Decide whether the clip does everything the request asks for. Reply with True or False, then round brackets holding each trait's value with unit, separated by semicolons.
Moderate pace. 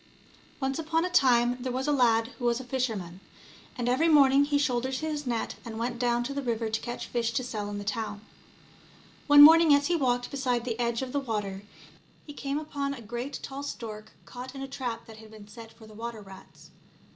False (225 wpm)